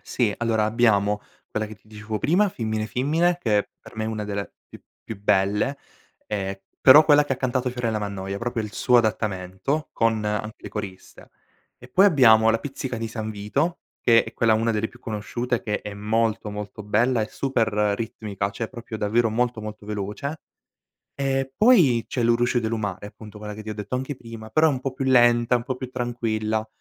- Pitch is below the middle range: Yes, low, 115 Hz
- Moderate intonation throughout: Yes, average, 3.0 semitones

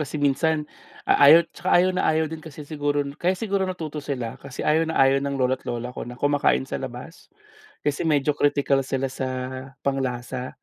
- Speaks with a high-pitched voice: No, medium, 145 Hz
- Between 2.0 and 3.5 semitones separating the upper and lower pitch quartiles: Yes, average, 3.0 semitones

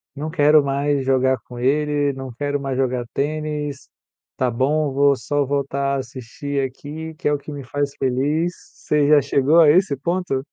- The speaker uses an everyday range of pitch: No, narrow, 2.0 semitones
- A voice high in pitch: No, medium, 140 Hz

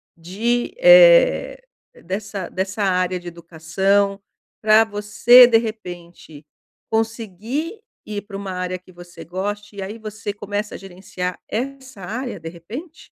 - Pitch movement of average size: Yes, average, 3.7 semitones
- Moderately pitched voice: No, high, 205 Hz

